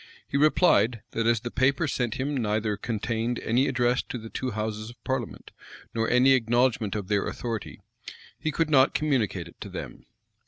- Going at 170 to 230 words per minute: Yes, average, 180 wpm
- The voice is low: Yes, low, 120 Hz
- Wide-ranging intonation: No, average, 3.0 semitones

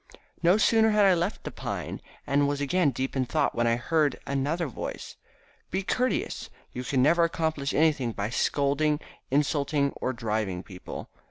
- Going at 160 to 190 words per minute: Yes, average, 165 wpm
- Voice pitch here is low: No, medium, 145 Hz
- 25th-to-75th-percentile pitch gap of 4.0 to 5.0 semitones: Yes, average, 4.6 semitones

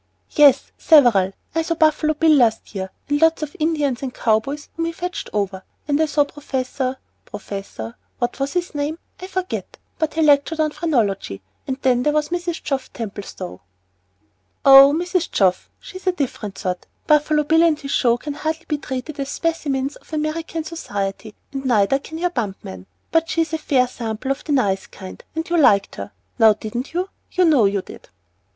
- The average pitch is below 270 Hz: No, very high, 285 Hz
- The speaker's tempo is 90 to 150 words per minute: No, average, 190 wpm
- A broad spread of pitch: Yes, wide, 6.1 semitones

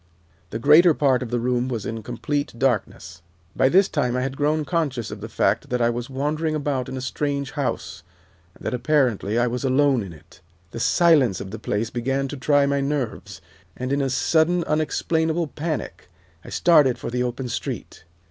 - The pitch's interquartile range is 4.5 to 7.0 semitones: No, average, 3.6 semitones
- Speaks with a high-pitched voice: No, low, 135 Hz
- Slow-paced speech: No, average, 195 wpm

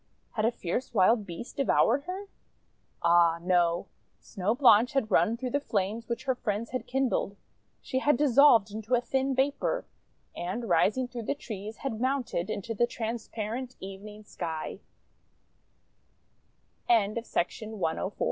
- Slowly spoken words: Yes, slow, 125 wpm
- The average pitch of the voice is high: Yes, high, 230 Hz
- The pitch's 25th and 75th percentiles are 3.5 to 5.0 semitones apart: Yes, average, 4.3 semitones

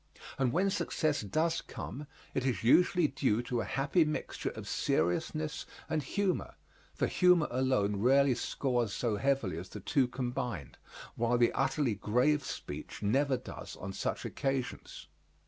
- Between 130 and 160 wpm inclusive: Yes, average, 145 wpm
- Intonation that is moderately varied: Yes, average, 4.2 semitones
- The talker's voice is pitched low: Yes, low, 130 Hz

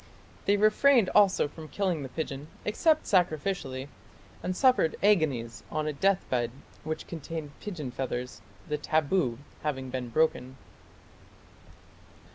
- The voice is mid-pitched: Yes, medium, 155 Hz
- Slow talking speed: Yes, slow, 115 wpm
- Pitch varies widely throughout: Yes, wide, 6.3 semitones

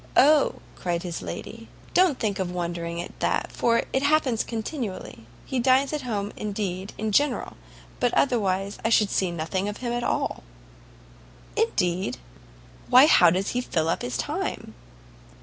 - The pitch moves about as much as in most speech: No, wide, 5.8 semitones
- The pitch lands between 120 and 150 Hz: No, high, 205 Hz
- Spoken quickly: No, average, 155 wpm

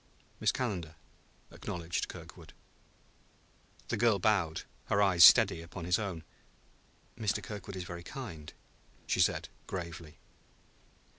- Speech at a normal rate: No, slow, 115 wpm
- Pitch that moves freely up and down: No, average, 3.6 semitones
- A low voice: Yes, very low, 90 Hz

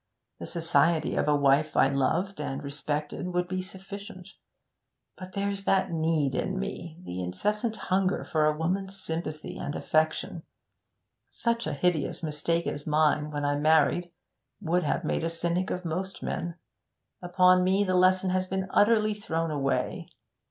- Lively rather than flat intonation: No, average, 3.6 semitones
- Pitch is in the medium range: Yes, medium, 175 Hz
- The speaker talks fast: No, average, 155 wpm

